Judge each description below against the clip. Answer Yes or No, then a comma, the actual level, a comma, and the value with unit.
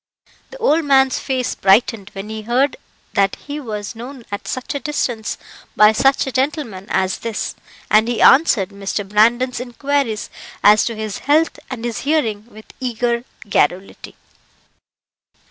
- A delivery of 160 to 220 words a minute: No, average, 145 wpm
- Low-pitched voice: No, high, 235 Hz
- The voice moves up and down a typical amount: Yes, average, 4.1 semitones